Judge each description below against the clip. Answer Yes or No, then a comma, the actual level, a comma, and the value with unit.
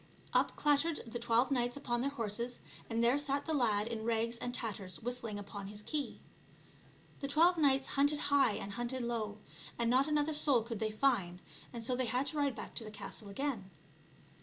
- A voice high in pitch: Yes, high, 240 Hz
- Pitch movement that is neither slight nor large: Yes, average, 4.0 semitones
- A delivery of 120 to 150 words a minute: No, average, 195 wpm